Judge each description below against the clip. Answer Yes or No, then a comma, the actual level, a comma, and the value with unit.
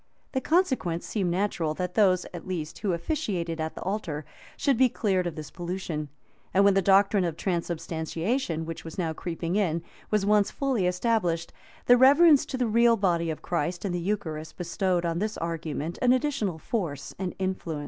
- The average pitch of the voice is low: No, medium, 180 Hz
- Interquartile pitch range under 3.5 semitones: No, average, 4.2 semitones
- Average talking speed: Yes, average, 180 wpm